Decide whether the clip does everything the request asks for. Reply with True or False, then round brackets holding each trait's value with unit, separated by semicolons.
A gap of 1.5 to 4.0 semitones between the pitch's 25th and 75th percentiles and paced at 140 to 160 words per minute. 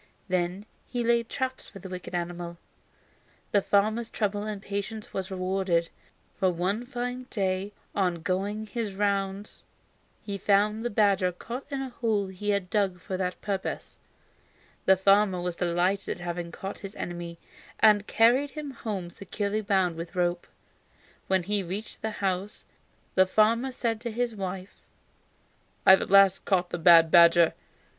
True (2.9 semitones; 155 wpm)